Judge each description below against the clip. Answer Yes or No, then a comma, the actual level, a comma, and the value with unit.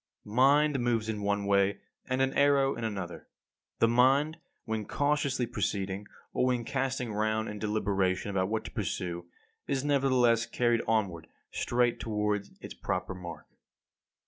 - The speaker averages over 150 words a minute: No, average, 145 wpm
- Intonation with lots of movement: No, average, 4.3 semitones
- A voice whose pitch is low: Yes, low, 110 Hz